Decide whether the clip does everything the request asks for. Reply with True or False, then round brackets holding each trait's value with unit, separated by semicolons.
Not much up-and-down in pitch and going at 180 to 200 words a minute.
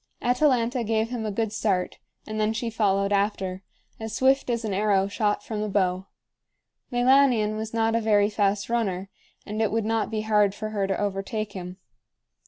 True (2.1 semitones; 185 wpm)